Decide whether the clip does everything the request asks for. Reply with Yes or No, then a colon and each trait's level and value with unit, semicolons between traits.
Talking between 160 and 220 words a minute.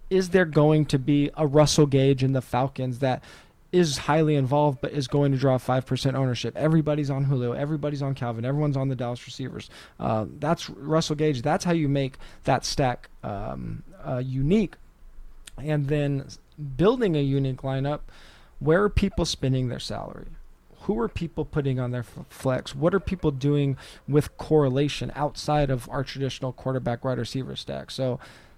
Yes: average, 170 wpm